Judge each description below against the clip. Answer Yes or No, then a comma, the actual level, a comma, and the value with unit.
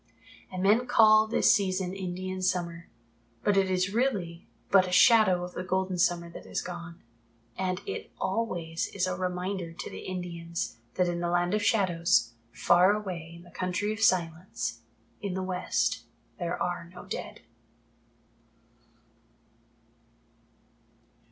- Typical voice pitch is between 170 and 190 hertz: Yes, medium, 185 Hz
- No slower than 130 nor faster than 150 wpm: Yes, average, 140 wpm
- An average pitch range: No, narrow, 1.9 semitones